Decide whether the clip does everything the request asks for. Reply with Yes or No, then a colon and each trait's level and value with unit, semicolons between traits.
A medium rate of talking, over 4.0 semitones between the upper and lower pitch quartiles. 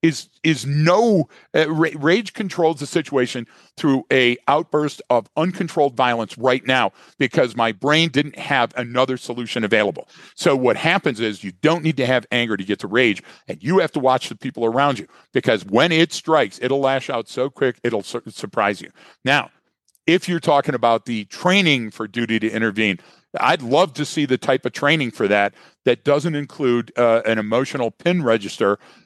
Yes: average, 185 wpm; average, 5.0 semitones